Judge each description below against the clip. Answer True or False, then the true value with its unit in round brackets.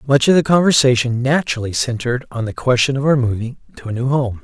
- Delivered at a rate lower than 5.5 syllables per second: False (6.4 syllables/s)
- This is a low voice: True (130 Hz)